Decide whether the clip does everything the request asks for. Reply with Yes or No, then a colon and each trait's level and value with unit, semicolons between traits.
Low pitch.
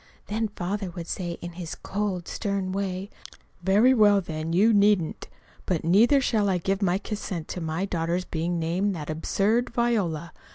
No: high, 190 Hz